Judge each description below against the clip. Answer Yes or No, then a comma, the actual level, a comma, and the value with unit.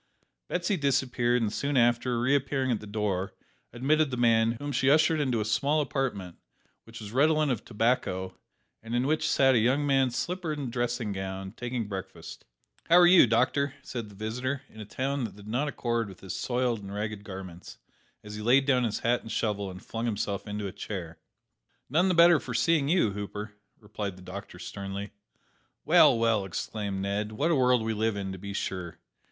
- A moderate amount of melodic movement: Yes, average, 4.6 semitones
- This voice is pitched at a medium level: No, low, 115 Hz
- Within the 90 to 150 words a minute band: No, average, 195 wpm